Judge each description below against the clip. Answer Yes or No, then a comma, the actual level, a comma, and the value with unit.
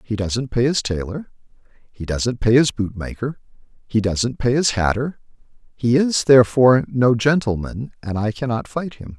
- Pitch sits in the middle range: No, low, 120 Hz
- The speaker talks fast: No, average, 165 wpm